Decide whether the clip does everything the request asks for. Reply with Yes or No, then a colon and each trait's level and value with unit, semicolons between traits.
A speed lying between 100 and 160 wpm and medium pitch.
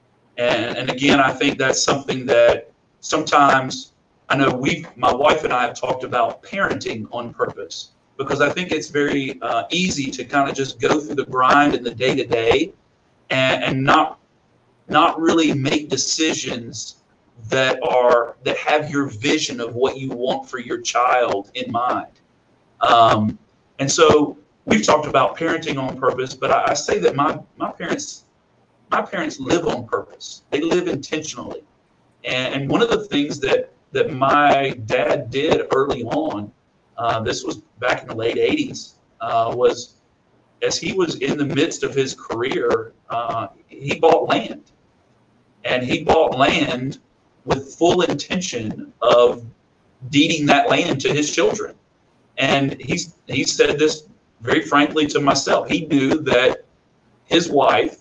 Yes: average, 155 wpm; medium, 150 Hz